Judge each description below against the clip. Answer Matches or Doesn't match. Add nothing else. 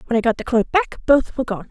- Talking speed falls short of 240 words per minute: Doesn't match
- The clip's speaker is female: Matches